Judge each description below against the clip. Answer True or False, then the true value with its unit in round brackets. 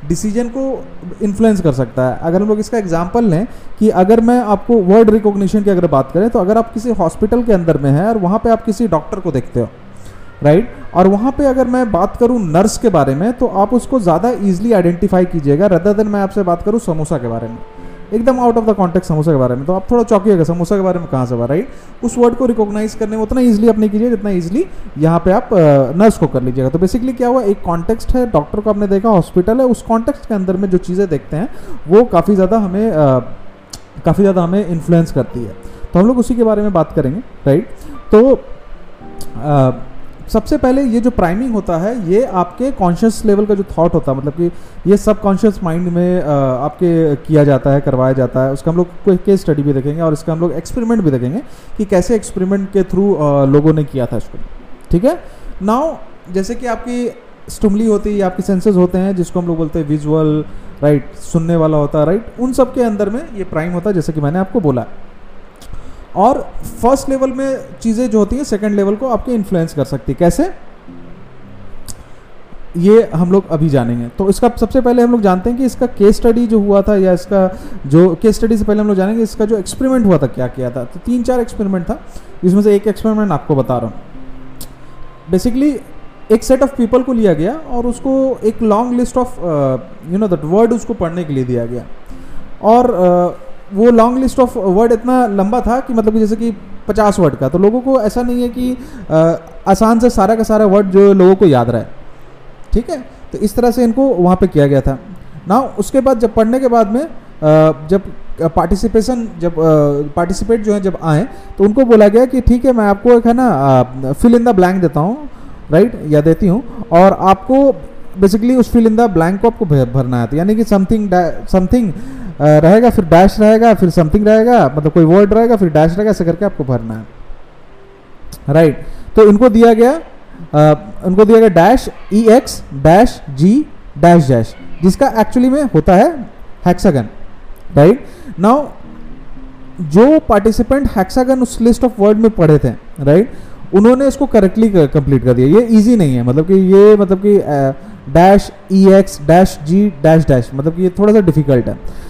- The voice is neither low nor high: False (195 Hz)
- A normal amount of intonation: False (6.0 semitones)